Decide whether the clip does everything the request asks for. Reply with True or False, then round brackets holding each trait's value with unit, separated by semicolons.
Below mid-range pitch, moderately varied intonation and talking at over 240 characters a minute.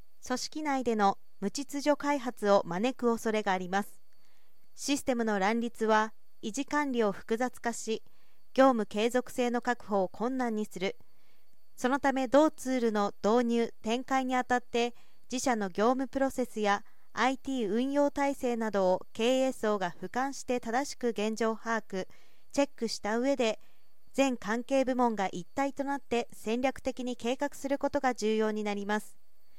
False (240 Hz; 3.5 semitones; 285 characters per minute)